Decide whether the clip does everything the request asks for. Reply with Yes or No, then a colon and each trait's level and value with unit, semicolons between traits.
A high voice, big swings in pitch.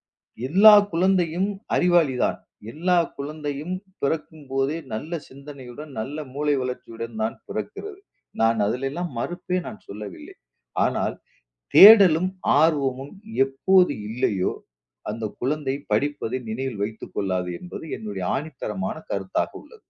No: medium, 145 Hz; wide, 6.1 semitones